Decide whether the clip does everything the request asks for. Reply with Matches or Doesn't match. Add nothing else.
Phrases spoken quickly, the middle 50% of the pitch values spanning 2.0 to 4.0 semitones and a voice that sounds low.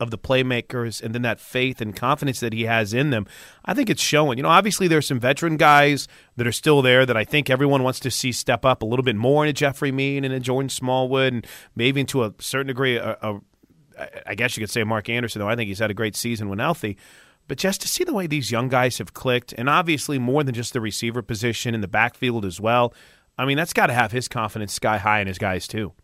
Matches